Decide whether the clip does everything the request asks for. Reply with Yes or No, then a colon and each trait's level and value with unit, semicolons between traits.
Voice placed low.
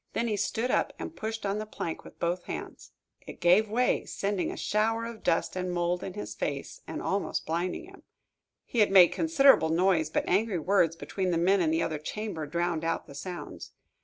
No: medium, 185 Hz